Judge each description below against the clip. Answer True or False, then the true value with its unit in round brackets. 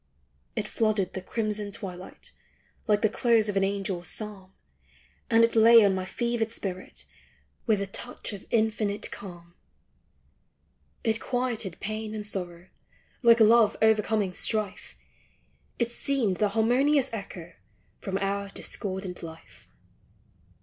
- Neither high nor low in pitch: False (210 Hz)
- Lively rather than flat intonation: False (2.9 semitones)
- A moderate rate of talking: False (125 wpm)